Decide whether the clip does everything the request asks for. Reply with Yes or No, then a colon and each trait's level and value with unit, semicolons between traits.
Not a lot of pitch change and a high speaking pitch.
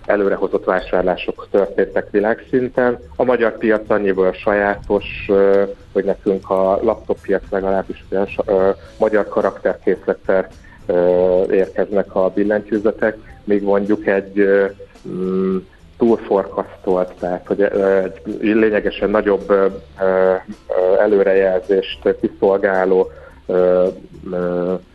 No: narrow, 1.9 semitones; very low, 95 Hz